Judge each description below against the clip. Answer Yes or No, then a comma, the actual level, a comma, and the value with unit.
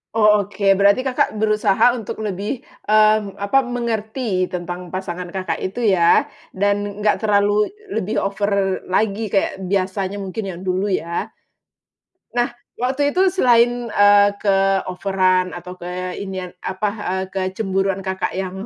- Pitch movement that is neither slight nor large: No, narrow, 2.3 semitones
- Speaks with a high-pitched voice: Yes, high, 200 Hz